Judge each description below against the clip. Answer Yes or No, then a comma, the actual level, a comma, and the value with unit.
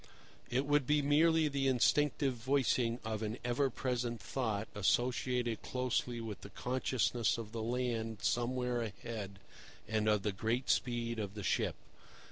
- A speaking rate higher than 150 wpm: No, average, 145 wpm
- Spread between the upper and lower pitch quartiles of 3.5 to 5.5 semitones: No, narrow, 2.6 semitones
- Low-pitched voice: Yes, low, 120 Hz